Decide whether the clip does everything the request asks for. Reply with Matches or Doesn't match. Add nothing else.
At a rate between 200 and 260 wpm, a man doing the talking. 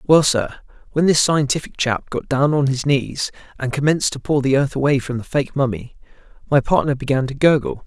Matches